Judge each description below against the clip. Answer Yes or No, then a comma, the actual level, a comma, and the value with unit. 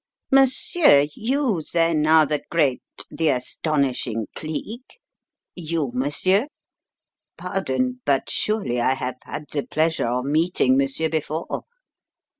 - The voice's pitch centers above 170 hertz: No, medium, 155 Hz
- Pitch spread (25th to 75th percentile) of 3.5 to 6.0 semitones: Yes, average, 5.0 semitones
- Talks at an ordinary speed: No, slow, 110 wpm